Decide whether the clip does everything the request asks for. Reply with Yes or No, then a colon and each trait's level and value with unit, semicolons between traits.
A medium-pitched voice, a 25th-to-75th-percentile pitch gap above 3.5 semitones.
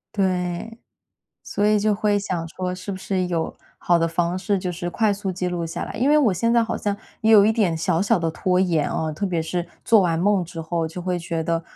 No: medium, 180 Hz; average, 3.2 semitones